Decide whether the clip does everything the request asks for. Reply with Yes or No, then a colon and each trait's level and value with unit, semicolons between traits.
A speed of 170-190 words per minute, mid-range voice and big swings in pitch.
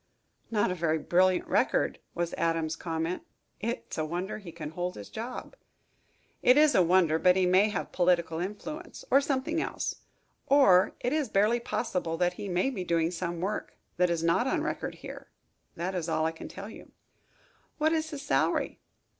Yes: average, 180 wpm; medium, 180 Hz; wide, 5.7 semitones